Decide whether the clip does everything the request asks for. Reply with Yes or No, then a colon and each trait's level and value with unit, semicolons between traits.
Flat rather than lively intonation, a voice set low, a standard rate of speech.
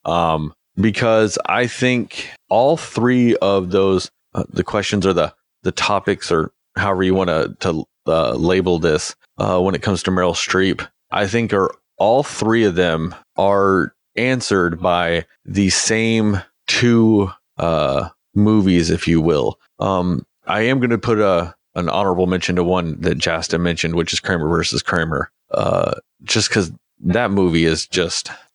No: average, 3.7 semitones; very low, 95 Hz; average, 160 wpm